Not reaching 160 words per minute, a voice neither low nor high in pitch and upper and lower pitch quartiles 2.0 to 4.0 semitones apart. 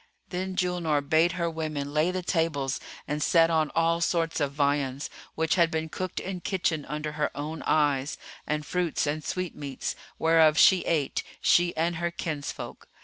No: average, 165 wpm; medium, 160 Hz; narrow, 2.5 semitones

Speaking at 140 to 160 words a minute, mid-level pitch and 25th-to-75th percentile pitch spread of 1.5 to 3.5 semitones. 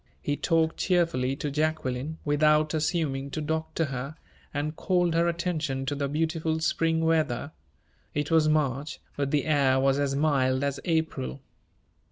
Yes: average, 150 wpm; medium, 150 Hz; narrow, 2.6 semitones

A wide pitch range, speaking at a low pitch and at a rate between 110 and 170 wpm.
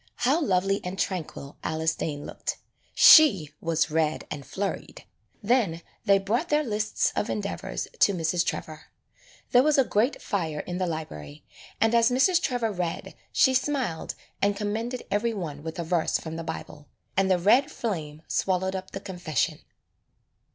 No: wide, 6.1 semitones; high, 190 Hz; average, 160 wpm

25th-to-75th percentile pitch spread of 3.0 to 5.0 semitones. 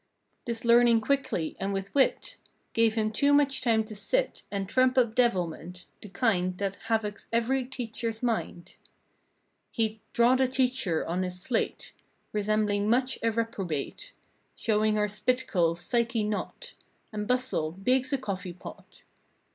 Yes: average, 4.1 semitones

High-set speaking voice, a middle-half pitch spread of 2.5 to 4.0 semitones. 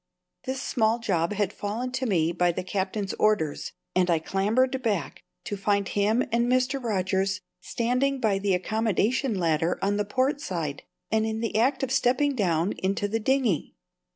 No: high, 210 Hz; average, 4.8 semitones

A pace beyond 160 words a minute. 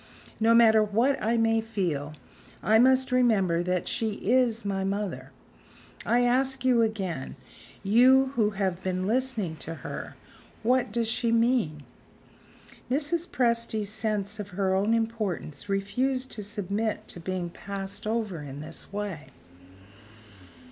No: slow, 135 wpm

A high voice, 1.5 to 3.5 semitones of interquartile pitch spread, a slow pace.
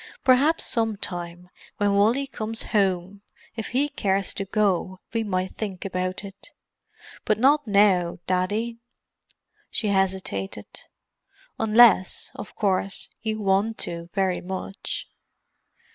Yes: high, 200 Hz; average, 3.1 semitones; slow, 115 wpm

